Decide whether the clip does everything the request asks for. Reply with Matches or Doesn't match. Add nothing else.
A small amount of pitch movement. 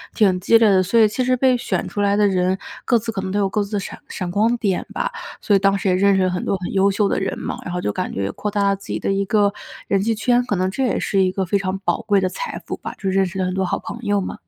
Matches